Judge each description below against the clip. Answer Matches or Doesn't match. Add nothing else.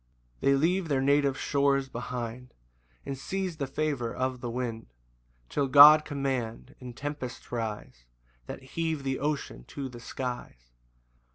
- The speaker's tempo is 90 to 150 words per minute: Matches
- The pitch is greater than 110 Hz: Matches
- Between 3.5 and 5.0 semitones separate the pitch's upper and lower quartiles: Doesn't match